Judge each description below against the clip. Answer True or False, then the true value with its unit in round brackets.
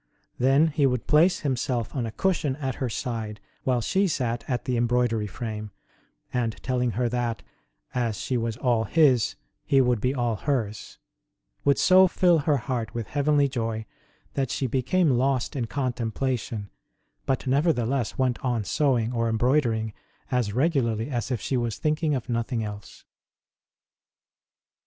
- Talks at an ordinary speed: True (155 wpm)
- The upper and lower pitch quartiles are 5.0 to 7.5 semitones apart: False (3.2 semitones)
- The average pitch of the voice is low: True (125 Hz)